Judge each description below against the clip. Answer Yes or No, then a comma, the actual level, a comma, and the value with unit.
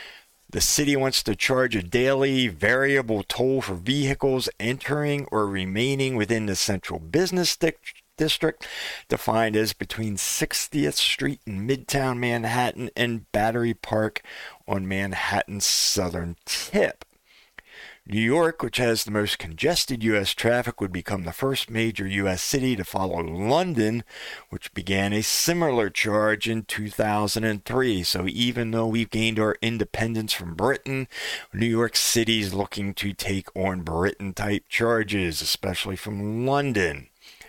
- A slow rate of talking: Yes, slow, 130 wpm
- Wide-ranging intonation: No, average, 3.9 semitones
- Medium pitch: No, low, 110 Hz